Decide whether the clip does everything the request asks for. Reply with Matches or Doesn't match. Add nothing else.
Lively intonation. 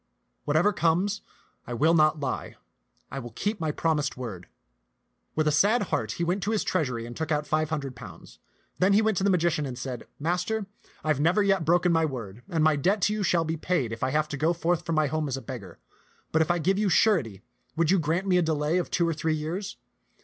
Doesn't match